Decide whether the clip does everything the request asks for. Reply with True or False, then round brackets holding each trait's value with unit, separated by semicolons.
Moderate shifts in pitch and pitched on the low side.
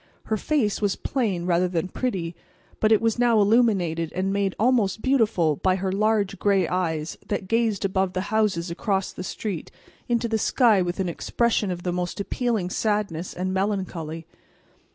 False (3.5 semitones; 195 Hz)